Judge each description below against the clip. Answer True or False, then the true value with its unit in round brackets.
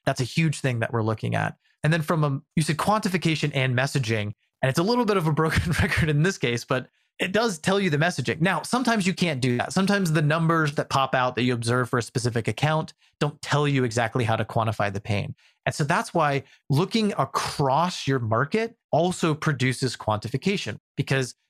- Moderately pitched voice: True (150 Hz)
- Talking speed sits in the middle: False (210 wpm)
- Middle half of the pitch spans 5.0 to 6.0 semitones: True (5.5 semitones)